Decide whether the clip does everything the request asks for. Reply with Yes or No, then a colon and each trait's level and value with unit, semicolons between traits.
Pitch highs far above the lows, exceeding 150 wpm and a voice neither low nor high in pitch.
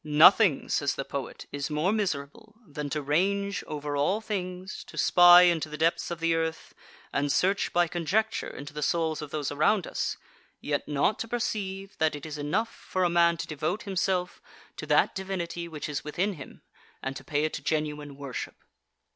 No: average, 4.3 semitones; average, 190 wpm; medium, 165 Hz